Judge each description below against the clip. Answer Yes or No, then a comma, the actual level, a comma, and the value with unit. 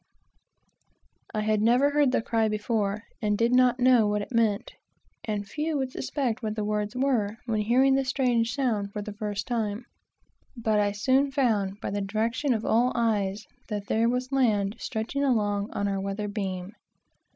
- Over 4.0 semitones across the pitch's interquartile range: No, average, 3.3 semitones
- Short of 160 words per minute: No, average, 175 wpm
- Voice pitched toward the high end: Yes, high, 220 Hz